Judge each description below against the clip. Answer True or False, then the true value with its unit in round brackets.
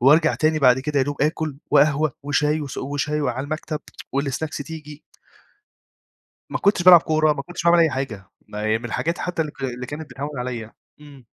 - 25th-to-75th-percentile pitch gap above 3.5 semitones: False (2.7 semitones)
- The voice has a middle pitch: True (145 Hz)